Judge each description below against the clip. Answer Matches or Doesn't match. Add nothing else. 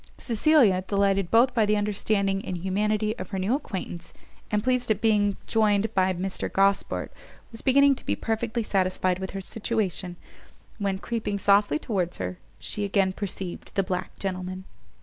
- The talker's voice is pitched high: Matches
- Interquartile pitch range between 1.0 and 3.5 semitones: Matches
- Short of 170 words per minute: Matches